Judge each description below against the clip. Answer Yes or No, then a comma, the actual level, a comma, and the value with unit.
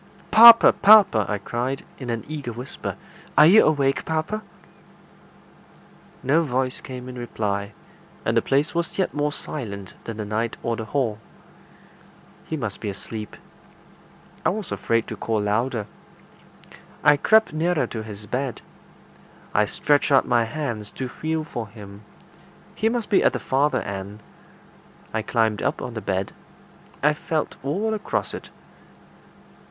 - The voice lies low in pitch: Yes, low, 125 Hz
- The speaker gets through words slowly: No, average, 145 wpm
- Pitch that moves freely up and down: Yes, wide, 6.0 semitones